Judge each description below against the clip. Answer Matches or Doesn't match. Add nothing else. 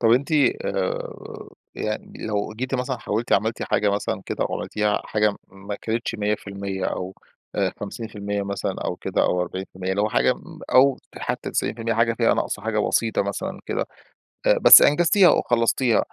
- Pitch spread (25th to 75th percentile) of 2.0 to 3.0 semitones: Matches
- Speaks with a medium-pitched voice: Doesn't match